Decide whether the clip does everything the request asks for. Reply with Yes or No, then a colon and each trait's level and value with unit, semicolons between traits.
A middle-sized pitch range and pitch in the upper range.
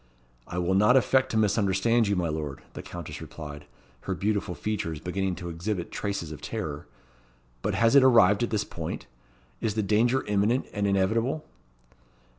No: average, 4.3 semitones; low, 100 Hz